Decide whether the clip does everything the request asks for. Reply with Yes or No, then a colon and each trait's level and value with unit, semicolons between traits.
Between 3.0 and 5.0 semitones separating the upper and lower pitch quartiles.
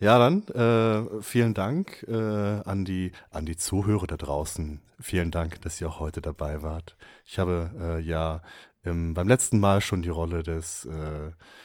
Yes: average, 4.6 semitones